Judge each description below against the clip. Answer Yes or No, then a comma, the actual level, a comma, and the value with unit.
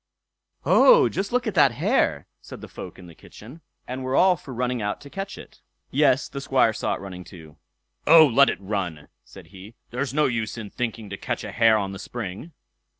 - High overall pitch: No, low, 120 Hz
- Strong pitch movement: Yes, wide, 6.0 semitones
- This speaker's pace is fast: Yes, fast, 210 wpm